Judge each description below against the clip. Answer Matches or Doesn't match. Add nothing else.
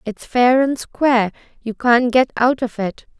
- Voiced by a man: Doesn't match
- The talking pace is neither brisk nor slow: Matches